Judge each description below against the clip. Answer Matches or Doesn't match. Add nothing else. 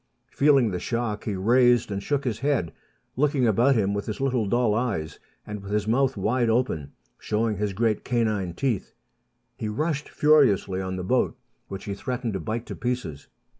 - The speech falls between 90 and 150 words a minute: Doesn't match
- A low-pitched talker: Matches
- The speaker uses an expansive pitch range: Doesn't match